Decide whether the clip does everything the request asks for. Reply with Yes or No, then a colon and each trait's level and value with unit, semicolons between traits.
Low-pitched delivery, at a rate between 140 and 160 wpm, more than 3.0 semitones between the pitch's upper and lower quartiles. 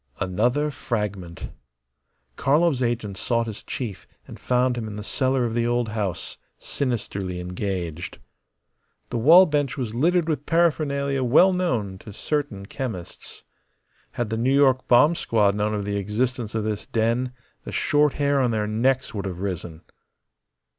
Yes: low, 120 Hz; average, 155 wpm; average, 5.0 semitones